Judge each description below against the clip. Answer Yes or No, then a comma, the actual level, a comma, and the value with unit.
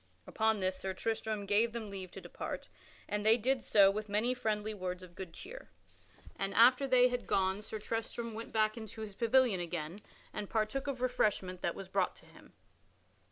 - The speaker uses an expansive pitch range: No, average, 3.1 semitones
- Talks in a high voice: Yes, high, 215 Hz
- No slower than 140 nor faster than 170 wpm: No, average, 190 wpm